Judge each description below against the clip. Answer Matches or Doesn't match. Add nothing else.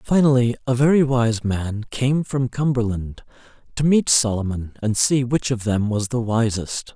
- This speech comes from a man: Matches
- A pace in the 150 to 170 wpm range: Matches